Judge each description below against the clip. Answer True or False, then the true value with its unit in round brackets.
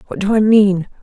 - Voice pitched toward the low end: False (205 Hz)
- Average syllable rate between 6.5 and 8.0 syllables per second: False (5.3 syllables/s)